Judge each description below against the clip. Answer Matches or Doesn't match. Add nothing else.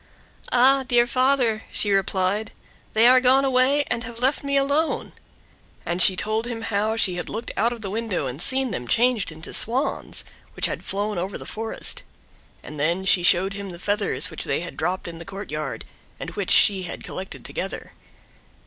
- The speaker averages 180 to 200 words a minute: Matches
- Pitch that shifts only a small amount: Doesn't match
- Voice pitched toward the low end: Doesn't match